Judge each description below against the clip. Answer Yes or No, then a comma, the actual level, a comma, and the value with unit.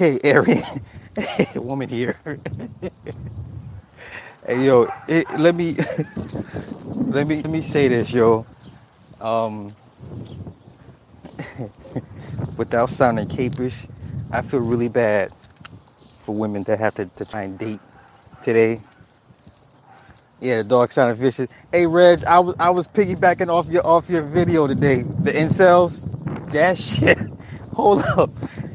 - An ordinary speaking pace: No, slow, 120 wpm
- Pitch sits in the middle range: No, low, 130 Hz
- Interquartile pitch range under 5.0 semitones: No, wide, 5.4 semitones